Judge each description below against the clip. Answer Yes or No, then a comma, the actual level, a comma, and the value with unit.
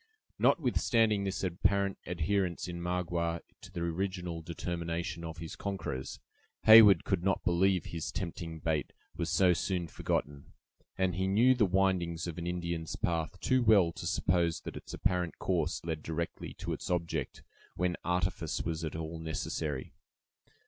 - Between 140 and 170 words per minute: Yes, average, 150 wpm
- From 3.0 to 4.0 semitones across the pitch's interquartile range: No, narrow, 2.4 semitones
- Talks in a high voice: No, very low, 85 Hz